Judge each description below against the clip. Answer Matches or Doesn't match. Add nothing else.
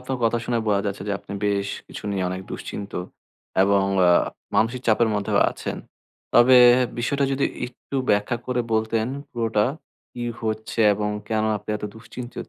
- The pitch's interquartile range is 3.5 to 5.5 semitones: Doesn't match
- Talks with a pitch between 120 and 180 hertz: Doesn't match